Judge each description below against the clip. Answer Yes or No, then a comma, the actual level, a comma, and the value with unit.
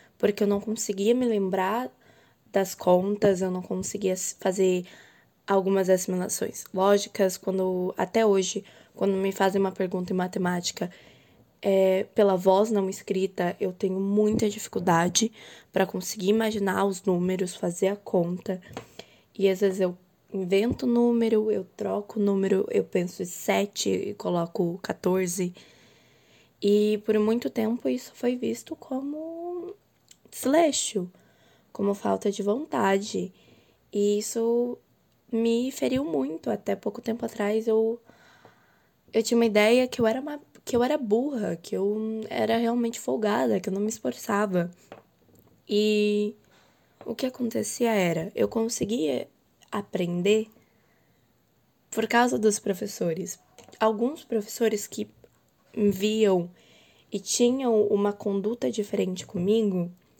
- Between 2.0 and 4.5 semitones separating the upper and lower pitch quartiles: Yes, average, 2.8 semitones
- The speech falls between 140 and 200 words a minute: No, average, 125 wpm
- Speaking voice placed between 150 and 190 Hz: No, high, 205 Hz